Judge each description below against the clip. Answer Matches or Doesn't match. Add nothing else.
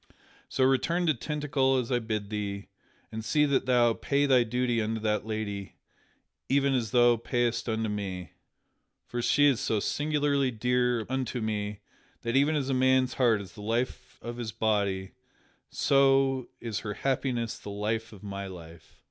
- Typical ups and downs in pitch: Matches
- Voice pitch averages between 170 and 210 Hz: Doesn't match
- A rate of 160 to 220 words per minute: Matches